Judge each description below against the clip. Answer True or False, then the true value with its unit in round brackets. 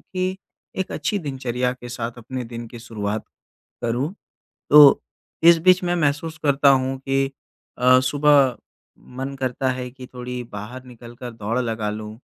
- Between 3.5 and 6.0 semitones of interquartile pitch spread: False (3.0 semitones)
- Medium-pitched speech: False (130 Hz)